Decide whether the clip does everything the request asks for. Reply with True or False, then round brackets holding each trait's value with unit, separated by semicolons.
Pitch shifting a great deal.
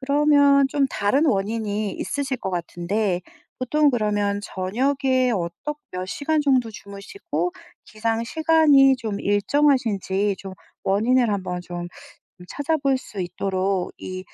True (6.1 semitones)